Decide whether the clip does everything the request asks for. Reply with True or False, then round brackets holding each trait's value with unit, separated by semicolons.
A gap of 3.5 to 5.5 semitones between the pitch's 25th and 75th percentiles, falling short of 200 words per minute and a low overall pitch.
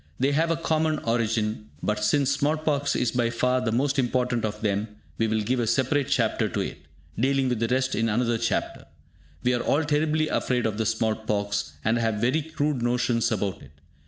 False (3.9 semitones; 205 wpm; 120 Hz)